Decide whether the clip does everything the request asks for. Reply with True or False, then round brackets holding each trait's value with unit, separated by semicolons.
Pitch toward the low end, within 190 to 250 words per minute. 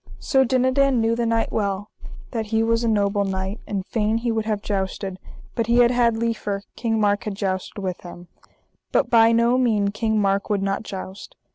False (220 Hz; 200 wpm)